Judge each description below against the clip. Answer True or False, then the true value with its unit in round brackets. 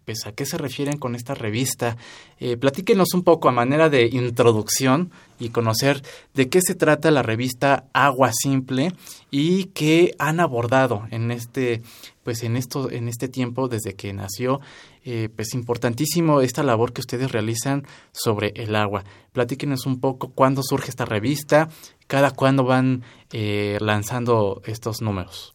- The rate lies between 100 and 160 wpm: True (155 wpm)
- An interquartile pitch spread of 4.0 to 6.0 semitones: False (3.3 semitones)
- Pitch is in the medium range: False (130 Hz)